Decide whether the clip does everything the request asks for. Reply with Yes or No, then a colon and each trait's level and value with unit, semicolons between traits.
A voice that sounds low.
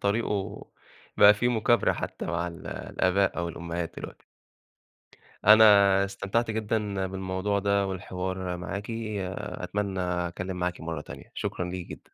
Yes: very low, 95 Hz